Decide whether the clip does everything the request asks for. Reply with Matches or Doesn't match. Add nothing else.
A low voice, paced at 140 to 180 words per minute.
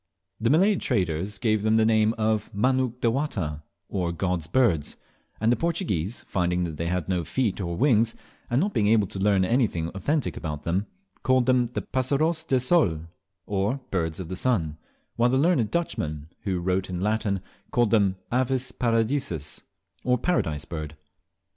Matches